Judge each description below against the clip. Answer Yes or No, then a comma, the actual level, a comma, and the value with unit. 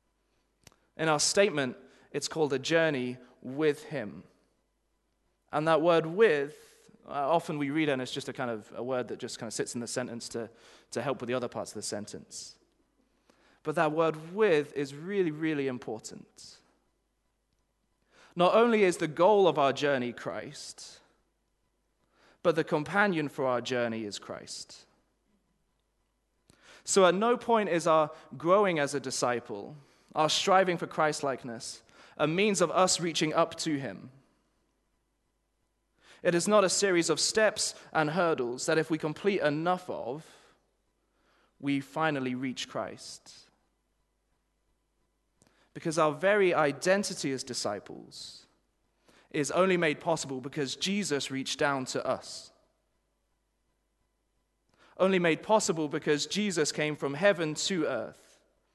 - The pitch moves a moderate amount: Yes, average, 4.5 semitones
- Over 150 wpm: No, slow, 135 wpm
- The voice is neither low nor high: Yes, medium, 155 Hz